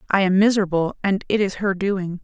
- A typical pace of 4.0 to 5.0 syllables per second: No, 5.7 syllables/s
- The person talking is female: Yes, female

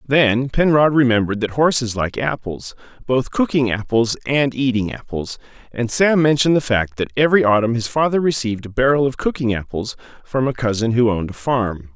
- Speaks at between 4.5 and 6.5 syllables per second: Yes, 5.5 syllables/s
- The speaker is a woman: No, male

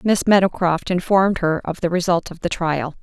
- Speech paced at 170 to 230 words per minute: Yes, average, 200 wpm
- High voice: No, medium, 175 Hz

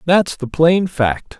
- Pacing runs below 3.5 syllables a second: Yes, 3.2 syllables/s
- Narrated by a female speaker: No, male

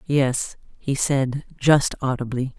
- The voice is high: No, low, 135 Hz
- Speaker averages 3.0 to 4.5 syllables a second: Yes, 3.3 syllables/s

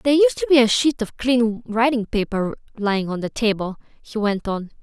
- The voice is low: No, high, 230 Hz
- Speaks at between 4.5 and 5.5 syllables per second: Yes, 5.3 syllables/s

